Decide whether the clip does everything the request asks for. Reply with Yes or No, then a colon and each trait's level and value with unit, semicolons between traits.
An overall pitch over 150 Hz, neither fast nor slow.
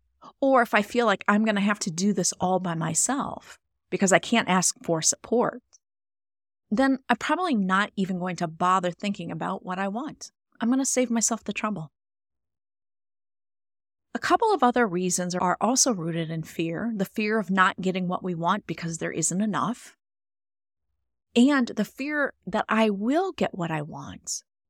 Yes: high, 190 Hz; average, 175 wpm